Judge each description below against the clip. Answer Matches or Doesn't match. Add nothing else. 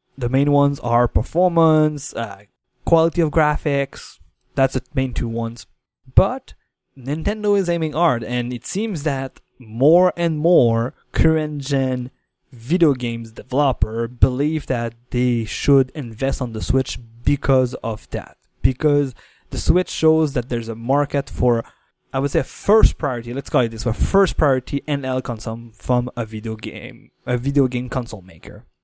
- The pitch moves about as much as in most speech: Matches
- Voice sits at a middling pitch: Doesn't match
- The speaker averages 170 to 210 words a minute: Doesn't match